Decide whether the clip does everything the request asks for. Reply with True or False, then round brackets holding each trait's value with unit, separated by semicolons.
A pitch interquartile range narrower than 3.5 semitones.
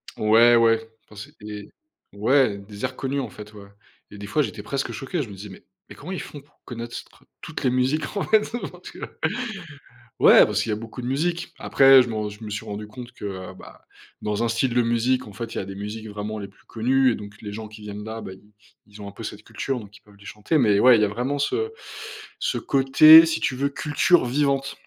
False (4.3 semitones)